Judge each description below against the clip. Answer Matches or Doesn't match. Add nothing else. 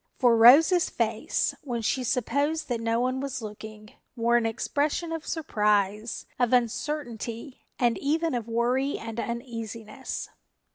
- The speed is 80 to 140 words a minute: Matches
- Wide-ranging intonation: Doesn't match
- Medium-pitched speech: Doesn't match